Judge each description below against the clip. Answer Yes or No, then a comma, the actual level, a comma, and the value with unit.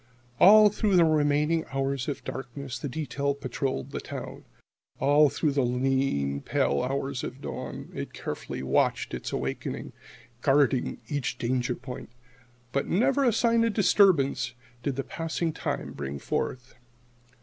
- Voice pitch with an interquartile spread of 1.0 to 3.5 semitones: No, average, 4.2 semitones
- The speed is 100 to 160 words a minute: Yes, average, 140 wpm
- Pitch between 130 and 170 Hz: Yes, medium, 140 Hz